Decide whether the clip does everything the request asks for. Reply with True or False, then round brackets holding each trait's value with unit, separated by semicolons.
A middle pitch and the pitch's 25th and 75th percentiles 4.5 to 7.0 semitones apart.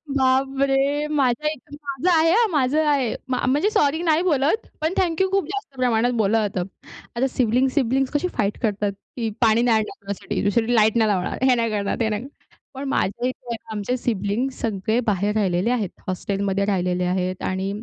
False (245 Hz; 5.2 semitones)